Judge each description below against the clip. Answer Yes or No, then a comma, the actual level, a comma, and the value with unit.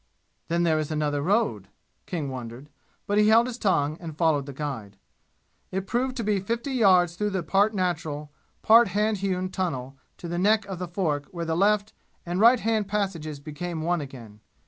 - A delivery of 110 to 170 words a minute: No, average, 185 wpm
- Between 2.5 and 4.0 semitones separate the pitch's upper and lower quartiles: No, wide, 5.5 semitones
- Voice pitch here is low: No, medium, 175 Hz